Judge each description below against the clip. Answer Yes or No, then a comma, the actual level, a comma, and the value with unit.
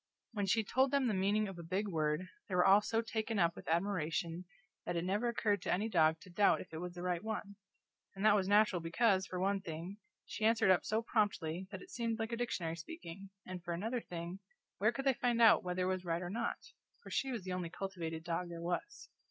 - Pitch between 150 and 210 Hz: Yes, high, 190 Hz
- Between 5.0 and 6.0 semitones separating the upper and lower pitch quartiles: No, average, 4.0 semitones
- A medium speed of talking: No, fast, 235 wpm